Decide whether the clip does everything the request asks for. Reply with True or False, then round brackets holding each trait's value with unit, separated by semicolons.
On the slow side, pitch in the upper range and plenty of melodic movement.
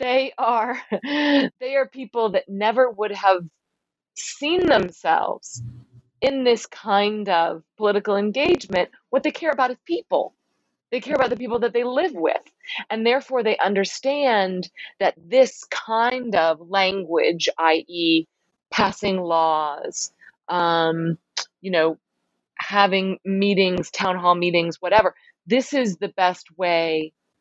True (125 wpm; 200 Hz; 6.9 semitones)